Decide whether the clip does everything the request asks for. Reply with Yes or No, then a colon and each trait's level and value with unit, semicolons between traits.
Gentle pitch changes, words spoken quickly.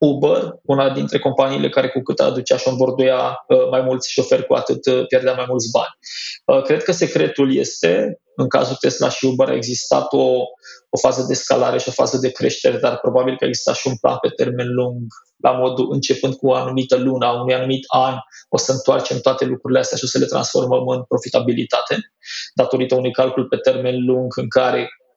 Yes: narrow, 0.7 semitones; fast, 195 wpm